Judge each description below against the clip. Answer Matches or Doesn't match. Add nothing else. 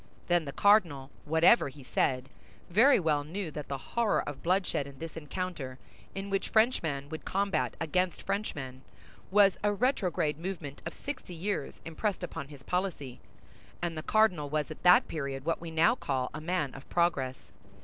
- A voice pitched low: Doesn't match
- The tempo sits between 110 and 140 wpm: Doesn't match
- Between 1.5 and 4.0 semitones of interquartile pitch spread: Doesn't match